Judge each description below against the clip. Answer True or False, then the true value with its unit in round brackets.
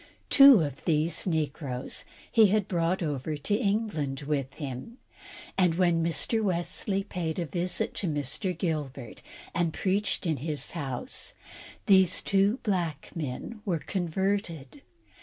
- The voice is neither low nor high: True (170 Hz)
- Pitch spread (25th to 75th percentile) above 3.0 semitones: True (4.7 semitones)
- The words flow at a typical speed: False (130 wpm)